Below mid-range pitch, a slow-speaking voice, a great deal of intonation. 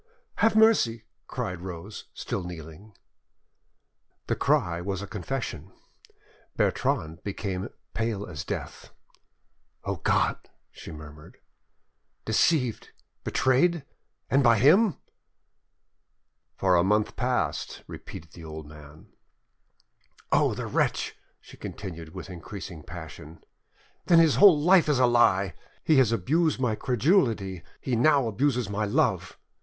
Yes: low, 105 Hz; slow, 115 wpm; wide, 7.4 semitones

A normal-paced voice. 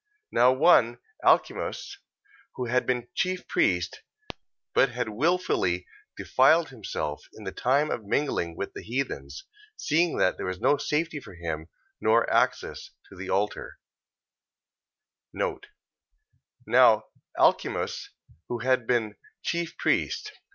No: slow, 120 wpm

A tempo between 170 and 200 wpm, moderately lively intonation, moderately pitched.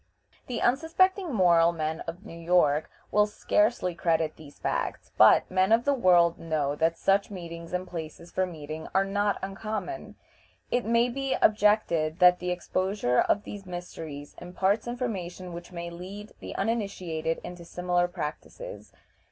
No: average, 150 wpm; average, 3.9 semitones; medium, 180 Hz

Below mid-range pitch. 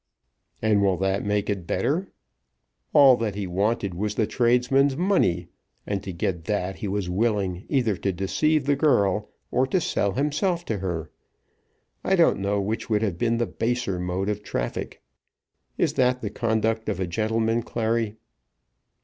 Yes: low, 105 Hz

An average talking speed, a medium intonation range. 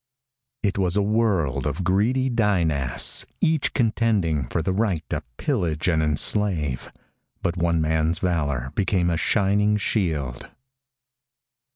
No: slow, 130 wpm; average, 5.0 semitones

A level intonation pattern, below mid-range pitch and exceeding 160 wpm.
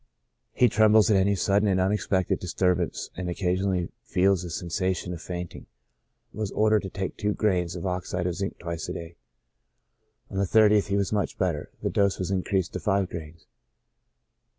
Yes: narrow, 2.2 semitones; very low, 95 Hz; average, 175 wpm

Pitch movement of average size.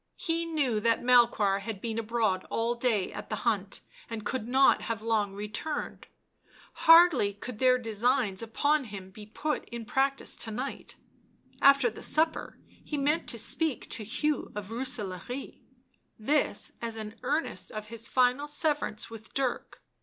Yes: average, 4.4 semitones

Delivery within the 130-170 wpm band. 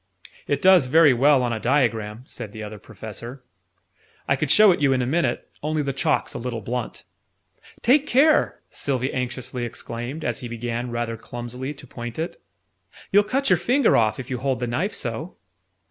No: average, 185 wpm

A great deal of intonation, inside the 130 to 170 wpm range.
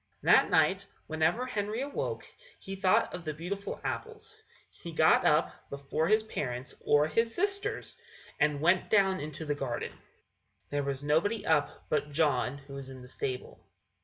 Yes: wide, 6.2 semitones; average, 160 wpm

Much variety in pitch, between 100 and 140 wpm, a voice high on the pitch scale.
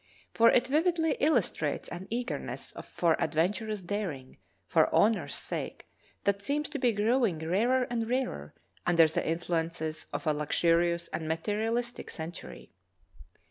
Yes: wide, 6.6 semitones; slow, 135 wpm; high, 200 Hz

